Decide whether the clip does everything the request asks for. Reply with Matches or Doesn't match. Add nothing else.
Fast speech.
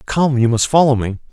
Matches